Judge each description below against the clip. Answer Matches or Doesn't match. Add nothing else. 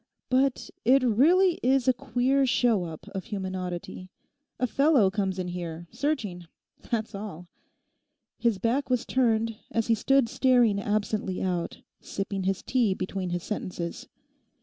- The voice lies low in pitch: Doesn't match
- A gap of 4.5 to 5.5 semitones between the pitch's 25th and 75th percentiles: Matches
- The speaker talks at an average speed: Matches